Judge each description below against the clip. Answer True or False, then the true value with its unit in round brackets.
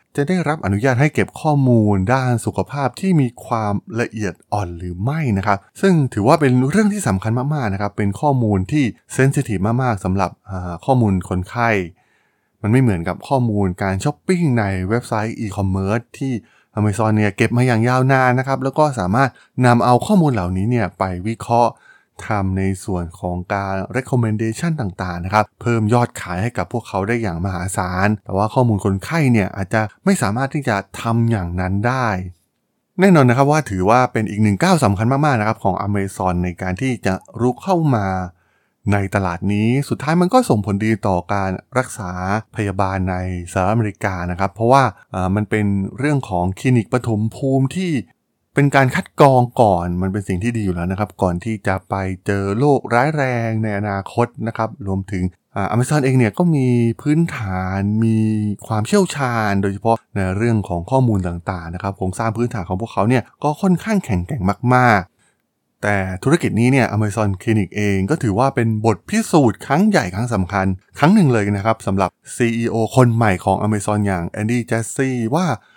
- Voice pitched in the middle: False (110 Hz)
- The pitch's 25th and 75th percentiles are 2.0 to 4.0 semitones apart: False (4.6 semitones)